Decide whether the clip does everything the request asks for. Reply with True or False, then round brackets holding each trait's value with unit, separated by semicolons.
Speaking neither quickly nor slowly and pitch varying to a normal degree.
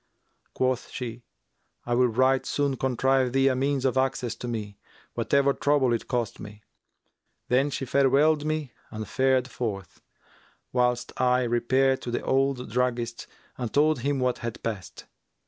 False (150 wpm; 2.0 semitones)